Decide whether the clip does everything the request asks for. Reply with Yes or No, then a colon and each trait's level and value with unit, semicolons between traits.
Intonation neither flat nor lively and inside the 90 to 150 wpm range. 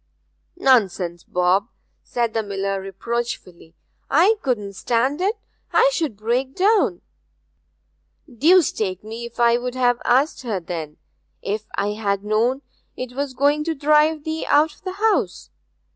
No: wide, 6.4 semitones; average, 140 wpm